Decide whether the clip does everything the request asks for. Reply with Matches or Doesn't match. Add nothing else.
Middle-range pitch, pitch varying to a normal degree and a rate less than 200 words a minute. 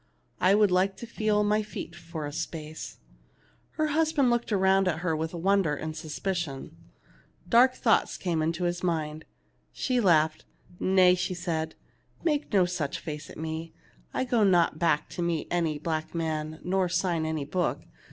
Matches